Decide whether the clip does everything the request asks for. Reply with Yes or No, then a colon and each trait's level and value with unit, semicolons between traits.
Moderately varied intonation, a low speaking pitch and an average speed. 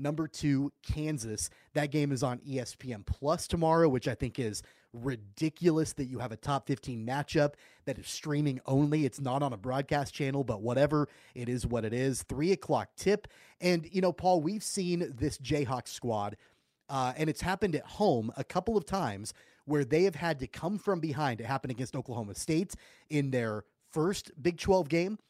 No: average, 4.2 semitones; medium, 145 Hz; average, 190 wpm